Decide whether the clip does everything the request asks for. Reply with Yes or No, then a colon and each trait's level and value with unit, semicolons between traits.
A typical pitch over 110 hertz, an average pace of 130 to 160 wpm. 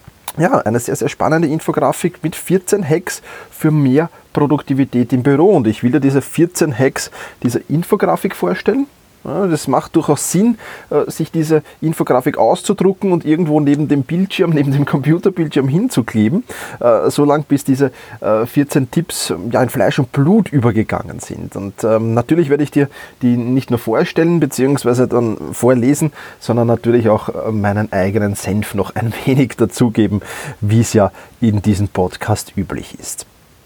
Yes: medium, 140 Hz; average, 145 wpm